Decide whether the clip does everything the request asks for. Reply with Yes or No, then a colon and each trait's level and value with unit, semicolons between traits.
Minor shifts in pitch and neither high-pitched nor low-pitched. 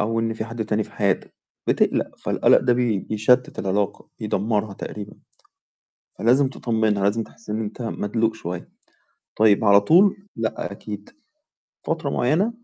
No: narrow, 2.3 semitones; low, 110 Hz